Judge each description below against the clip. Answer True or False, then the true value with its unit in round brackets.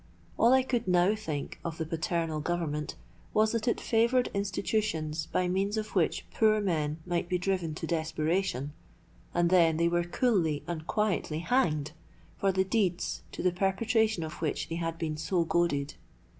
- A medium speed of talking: True (170 wpm)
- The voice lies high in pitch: False (175 Hz)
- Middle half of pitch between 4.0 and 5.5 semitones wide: True (4.3 semitones)